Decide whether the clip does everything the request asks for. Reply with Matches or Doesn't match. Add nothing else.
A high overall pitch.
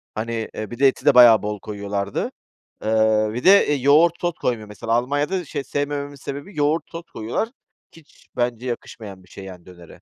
Doesn't match